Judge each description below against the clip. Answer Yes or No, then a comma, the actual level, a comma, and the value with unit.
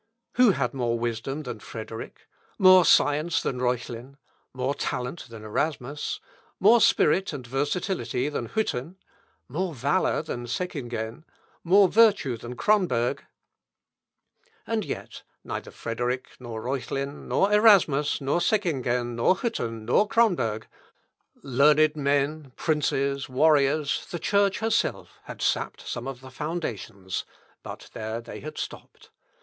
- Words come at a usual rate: No, slow, 120 wpm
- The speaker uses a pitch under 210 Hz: Yes, medium, 140 Hz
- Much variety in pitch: Yes, wide, 6.1 semitones